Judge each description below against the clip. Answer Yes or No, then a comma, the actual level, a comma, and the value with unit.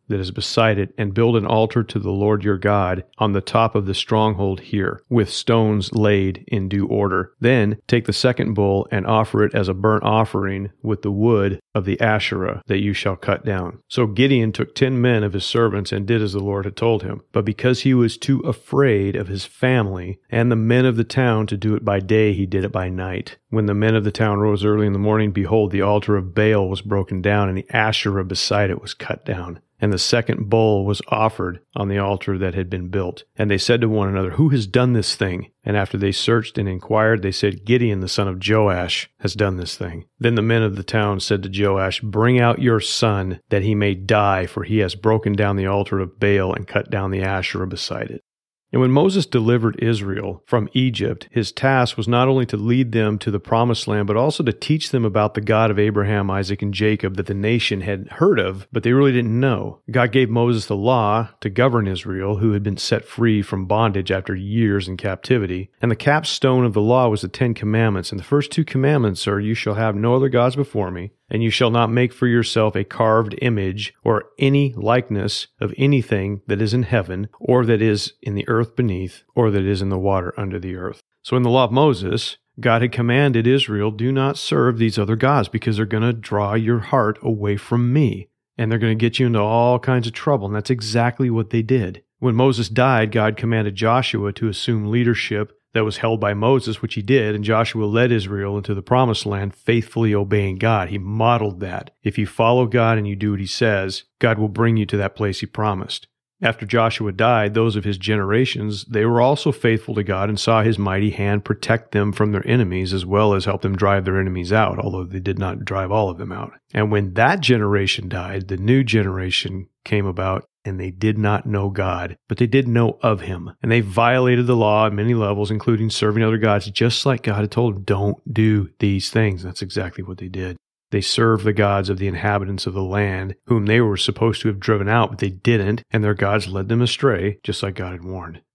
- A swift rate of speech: Yes, fast, 230 wpm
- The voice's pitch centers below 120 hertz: Yes, low, 105 Hz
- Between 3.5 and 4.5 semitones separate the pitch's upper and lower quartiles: No, average, 2.7 semitones